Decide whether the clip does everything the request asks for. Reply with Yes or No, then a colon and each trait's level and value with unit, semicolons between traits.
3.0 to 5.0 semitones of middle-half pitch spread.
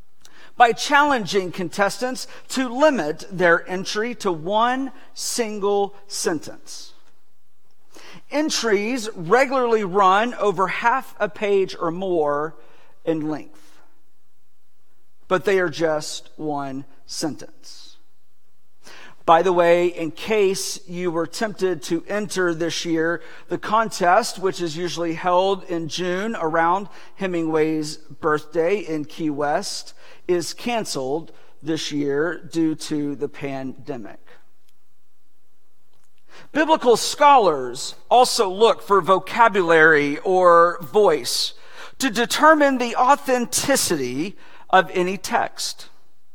No: wide, 5.6 semitones